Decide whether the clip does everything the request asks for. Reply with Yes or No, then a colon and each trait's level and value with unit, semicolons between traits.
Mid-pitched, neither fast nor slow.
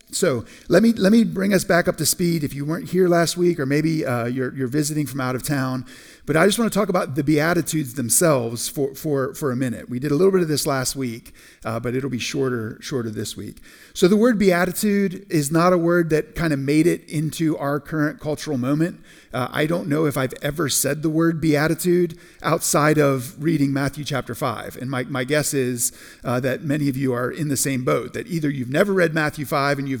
No: medium, 150 Hz; fast, 235 wpm